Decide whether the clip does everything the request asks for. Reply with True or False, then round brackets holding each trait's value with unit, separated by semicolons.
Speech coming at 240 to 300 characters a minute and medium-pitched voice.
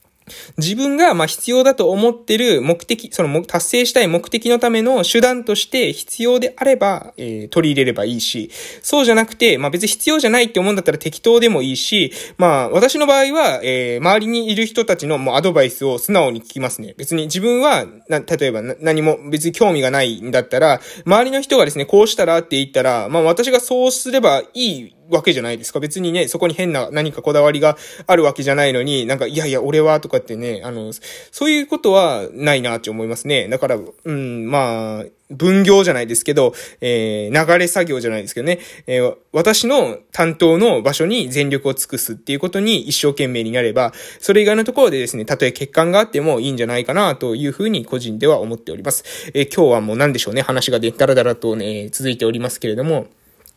False (415 characters per minute; 160 Hz)